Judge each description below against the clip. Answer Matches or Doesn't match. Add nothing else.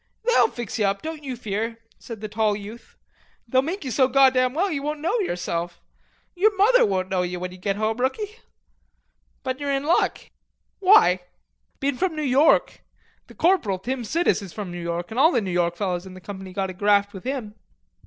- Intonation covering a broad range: Matches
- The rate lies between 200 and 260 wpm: Matches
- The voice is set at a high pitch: Matches